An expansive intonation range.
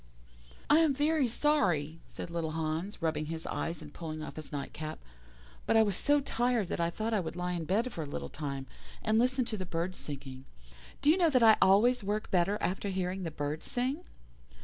Yes: wide, 6.9 semitones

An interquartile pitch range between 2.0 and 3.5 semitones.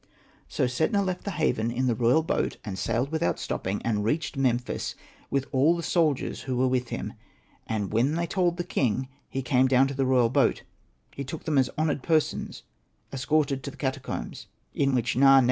No: average, 4.0 semitones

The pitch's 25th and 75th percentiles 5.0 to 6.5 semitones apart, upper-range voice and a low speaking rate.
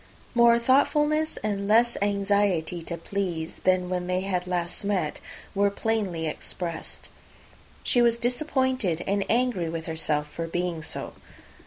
Yes: wide, 5.5 semitones; high, 195 Hz; slow, 130 wpm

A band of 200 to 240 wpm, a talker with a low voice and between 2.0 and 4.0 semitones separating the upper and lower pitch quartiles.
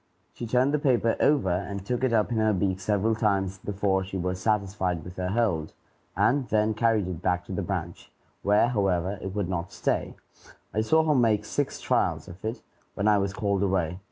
Yes: fast, 205 wpm; low, 100 Hz; average, 3.0 semitones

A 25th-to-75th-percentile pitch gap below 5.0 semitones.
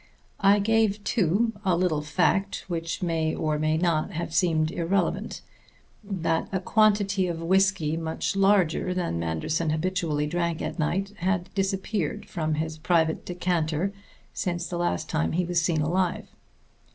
Yes: average, 3.3 semitones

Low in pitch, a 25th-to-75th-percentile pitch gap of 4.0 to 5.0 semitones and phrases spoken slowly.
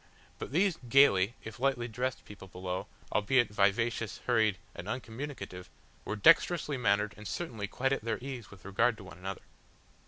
No: low, 110 Hz; average, 4.6 semitones; average, 160 wpm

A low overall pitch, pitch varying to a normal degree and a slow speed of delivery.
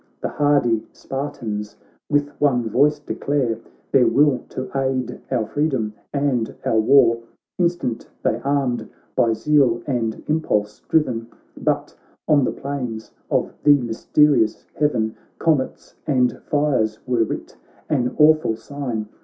Yes: low, 130 Hz; average, 4.2 semitones; slow, 125 wpm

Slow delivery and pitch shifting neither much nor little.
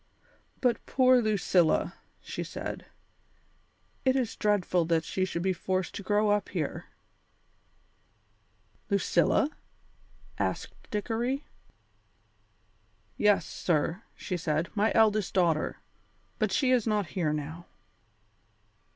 Yes: slow, 105 wpm; average, 4.3 semitones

